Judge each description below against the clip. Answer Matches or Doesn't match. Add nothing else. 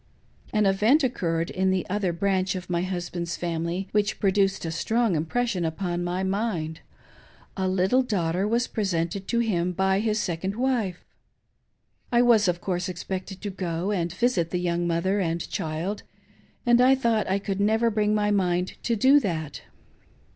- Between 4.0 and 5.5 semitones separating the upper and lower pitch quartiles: Doesn't match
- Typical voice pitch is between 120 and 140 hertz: Doesn't match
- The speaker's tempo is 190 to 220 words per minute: Doesn't match